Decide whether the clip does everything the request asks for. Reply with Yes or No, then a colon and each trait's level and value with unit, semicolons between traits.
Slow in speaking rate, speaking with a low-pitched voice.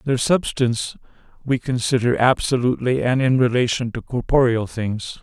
Yes: slow, 125 wpm; low, 125 Hz